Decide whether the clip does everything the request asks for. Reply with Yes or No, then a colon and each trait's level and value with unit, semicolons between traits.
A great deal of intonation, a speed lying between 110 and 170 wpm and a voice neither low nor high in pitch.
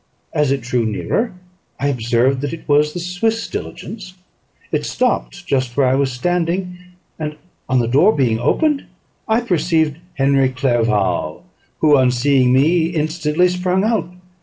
Yes: wide, 5.7 semitones; average, 150 wpm; medium, 145 Hz